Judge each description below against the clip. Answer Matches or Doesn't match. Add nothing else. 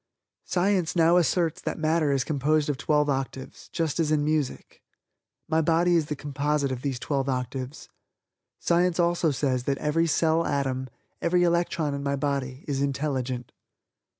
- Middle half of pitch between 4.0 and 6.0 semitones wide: Doesn't match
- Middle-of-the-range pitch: Matches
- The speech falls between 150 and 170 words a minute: Matches